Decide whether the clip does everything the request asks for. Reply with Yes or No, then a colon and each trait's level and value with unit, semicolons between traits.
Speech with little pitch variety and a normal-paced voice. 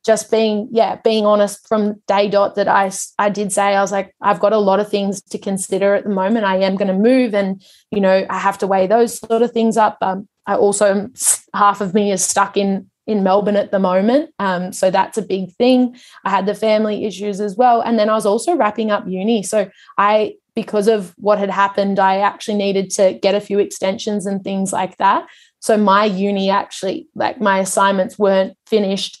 No: narrow, 1.9 semitones; fast, 220 wpm